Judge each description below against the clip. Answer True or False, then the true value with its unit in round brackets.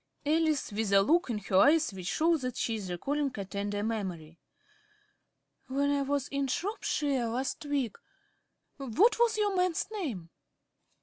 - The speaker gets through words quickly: False (150 wpm)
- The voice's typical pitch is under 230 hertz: False (270 Hz)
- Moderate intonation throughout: False (7.3 semitones)